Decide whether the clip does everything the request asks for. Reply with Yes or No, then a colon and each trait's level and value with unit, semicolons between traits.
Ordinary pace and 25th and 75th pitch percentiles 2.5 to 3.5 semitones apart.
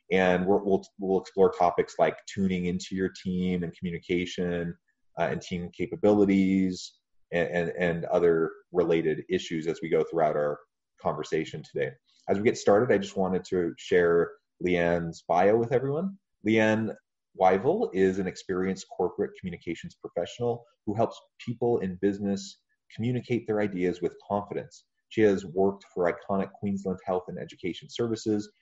Yes: average, 145 wpm; average, 3.2 semitones